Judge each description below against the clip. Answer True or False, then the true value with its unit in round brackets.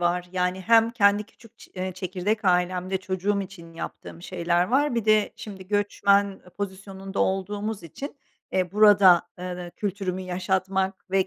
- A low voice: False (190 Hz)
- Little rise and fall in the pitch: True (2.1 semitones)